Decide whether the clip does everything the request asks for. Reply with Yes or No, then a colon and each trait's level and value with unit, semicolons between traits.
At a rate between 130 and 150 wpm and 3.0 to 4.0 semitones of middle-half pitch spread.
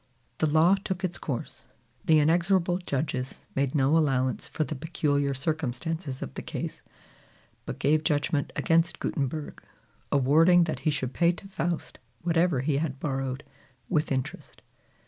Yes: average, 145 wpm; average, 3.4 semitones